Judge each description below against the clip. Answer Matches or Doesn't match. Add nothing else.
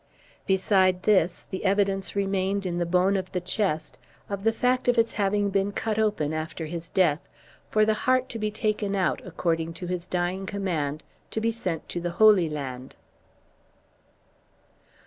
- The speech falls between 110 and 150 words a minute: Doesn't match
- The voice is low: Doesn't match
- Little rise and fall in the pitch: Doesn't match